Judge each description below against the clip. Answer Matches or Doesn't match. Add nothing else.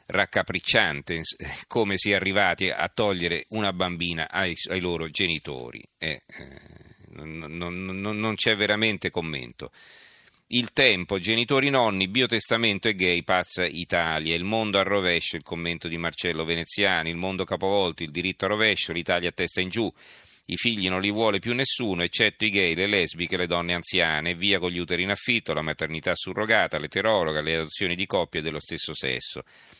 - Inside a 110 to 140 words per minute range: Doesn't match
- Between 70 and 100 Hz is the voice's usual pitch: Matches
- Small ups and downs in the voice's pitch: Doesn't match